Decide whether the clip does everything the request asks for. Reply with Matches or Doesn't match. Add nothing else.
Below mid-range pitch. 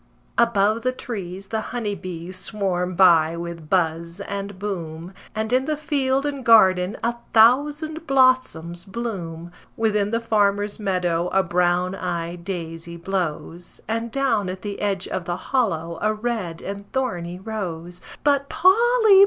Doesn't match